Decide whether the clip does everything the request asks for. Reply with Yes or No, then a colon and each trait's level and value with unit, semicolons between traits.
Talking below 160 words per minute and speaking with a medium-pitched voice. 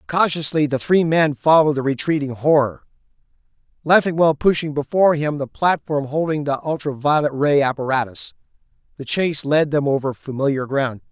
Yes: average, 145 wpm; medium, 145 Hz